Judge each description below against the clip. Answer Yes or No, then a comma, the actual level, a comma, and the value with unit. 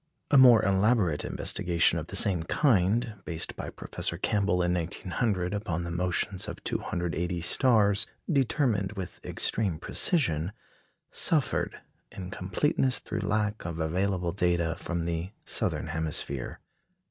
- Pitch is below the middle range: Yes, very low, 90 Hz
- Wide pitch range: No, average, 3.9 semitones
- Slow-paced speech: Yes, slow, 125 wpm